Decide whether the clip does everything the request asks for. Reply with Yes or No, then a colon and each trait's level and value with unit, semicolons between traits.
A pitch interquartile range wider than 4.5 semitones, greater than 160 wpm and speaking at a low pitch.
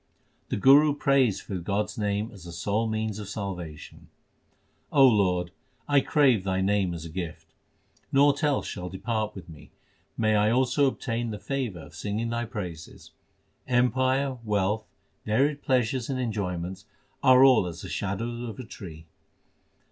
No: average, 5.2 semitones; average, 155 wpm; low, 110 Hz